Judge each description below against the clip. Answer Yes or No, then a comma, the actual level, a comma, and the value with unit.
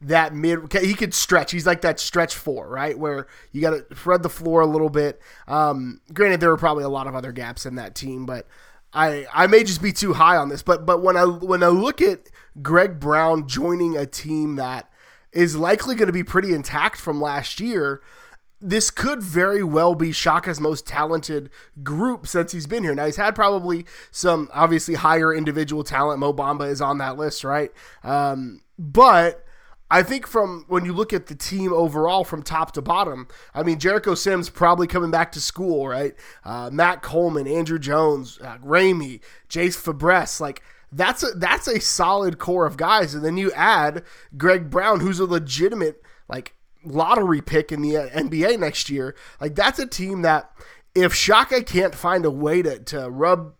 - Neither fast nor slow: Yes, average, 190 wpm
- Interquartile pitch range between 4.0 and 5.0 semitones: No, average, 3.5 semitones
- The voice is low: No, medium, 165 Hz